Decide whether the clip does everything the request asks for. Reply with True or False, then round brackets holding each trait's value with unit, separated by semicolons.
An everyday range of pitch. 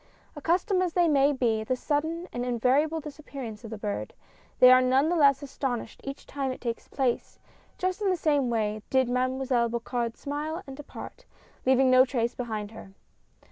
True (3.6 semitones)